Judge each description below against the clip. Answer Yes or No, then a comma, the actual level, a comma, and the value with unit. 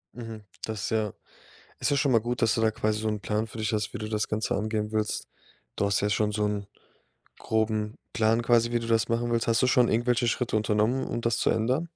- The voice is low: Yes, low, 110 Hz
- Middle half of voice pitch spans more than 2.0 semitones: No, narrow, 1.7 semitones